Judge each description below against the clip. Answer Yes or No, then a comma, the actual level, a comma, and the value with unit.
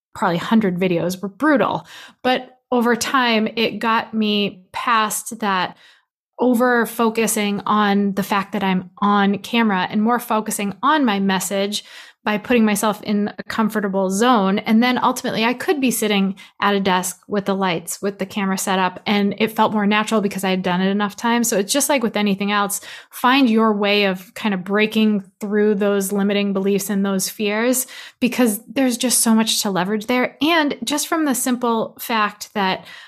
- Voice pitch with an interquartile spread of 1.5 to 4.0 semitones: Yes, average, 2.8 semitones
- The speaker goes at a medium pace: Yes, average, 185 wpm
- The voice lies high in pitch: Yes, high, 210 Hz